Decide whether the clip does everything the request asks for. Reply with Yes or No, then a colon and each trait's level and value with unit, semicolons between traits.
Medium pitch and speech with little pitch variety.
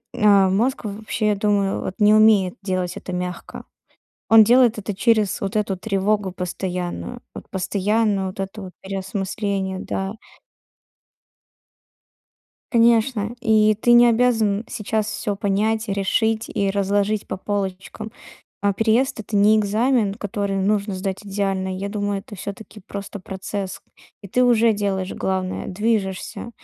No: high, 205 Hz; narrow, 2.1 semitones